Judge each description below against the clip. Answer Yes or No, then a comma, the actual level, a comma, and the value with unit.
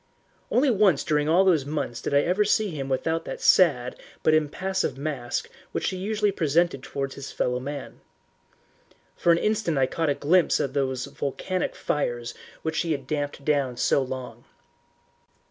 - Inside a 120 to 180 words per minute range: Yes, average, 165 wpm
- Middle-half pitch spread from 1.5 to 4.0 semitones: No, average, 4.7 semitones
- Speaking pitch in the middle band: Yes, medium, 150 Hz